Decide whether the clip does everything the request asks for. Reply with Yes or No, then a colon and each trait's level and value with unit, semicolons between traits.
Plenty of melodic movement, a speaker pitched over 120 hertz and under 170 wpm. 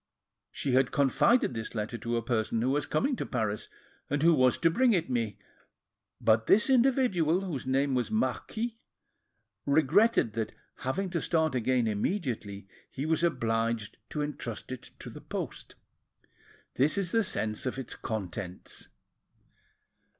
Yes: wide, 7.1 semitones; low, 135 Hz; average, 150 wpm